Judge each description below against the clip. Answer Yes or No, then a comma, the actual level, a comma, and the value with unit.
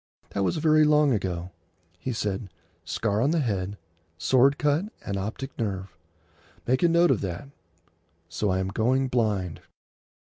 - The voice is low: Yes, low, 110 Hz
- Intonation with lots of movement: Yes, wide, 6.5 semitones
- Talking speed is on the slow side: No, average, 145 wpm